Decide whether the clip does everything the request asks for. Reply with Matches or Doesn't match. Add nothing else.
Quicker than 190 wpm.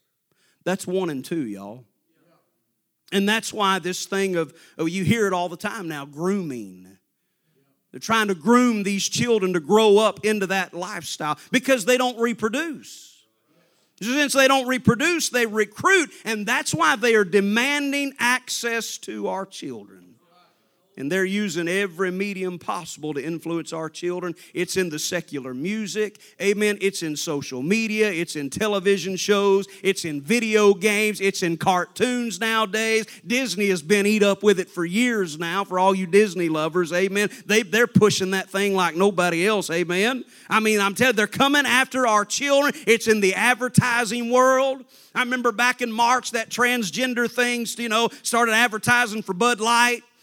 Doesn't match